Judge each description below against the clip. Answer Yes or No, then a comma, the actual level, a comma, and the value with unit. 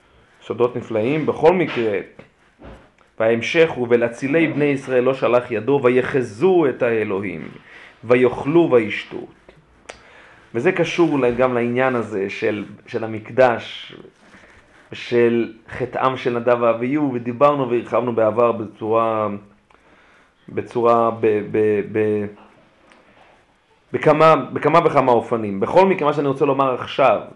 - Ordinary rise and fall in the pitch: Yes, average, 3.6 semitones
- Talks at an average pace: Yes, average, 110 wpm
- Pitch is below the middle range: Yes, low, 120 Hz